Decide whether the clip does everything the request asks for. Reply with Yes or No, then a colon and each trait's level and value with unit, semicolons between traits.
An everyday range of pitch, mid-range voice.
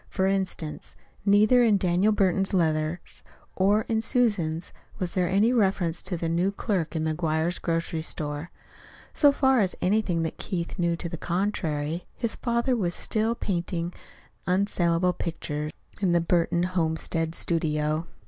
Yes: average, 3.4 semitones; medium, 175 Hz